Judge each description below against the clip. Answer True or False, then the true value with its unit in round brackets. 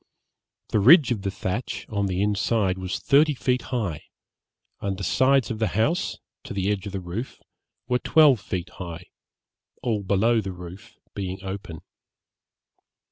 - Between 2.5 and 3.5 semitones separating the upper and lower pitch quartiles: False (4.2 semitones)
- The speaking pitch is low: True (100 Hz)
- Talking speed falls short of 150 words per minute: False (155 wpm)